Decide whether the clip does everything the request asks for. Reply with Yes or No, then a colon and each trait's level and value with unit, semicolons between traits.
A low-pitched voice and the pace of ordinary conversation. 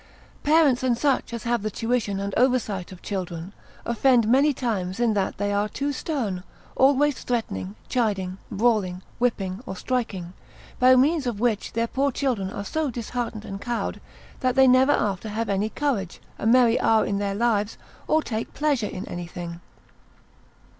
No: high, 225 Hz; average, 165 wpm